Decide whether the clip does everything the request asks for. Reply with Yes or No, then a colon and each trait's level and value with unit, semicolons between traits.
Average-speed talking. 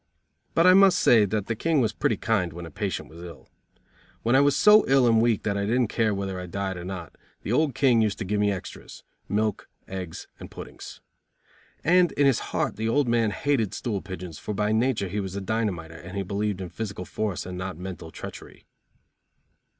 No: fast, 210 wpm